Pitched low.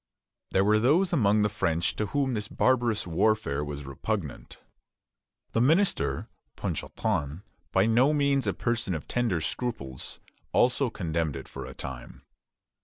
Yes: low, 105 Hz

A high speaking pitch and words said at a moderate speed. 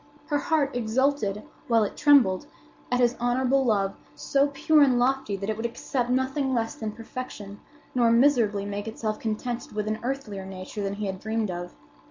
Yes: high, 230 Hz; average, 175 wpm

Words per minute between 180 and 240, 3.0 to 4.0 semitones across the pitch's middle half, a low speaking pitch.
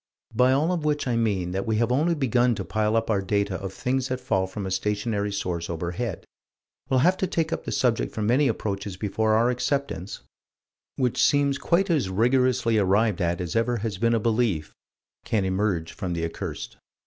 No: average, 195 wpm; average, 4.7 semitones; low, 110 Hz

